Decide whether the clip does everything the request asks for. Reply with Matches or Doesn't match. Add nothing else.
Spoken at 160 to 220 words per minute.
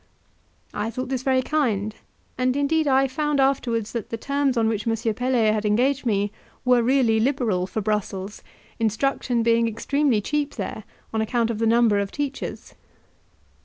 Matches